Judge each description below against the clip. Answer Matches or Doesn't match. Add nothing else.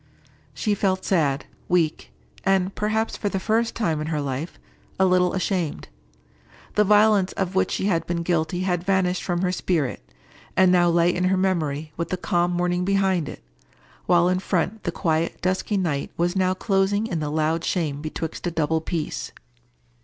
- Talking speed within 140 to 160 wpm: Doesn't match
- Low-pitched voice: Doesn't match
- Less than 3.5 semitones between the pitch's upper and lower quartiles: Matches